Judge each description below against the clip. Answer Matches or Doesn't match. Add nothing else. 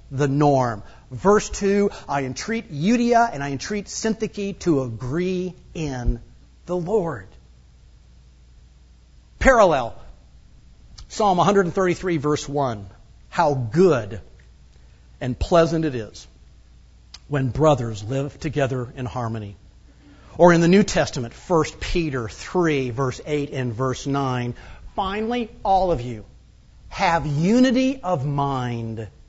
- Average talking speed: Doesn't match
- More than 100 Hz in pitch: Matches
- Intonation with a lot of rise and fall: Matches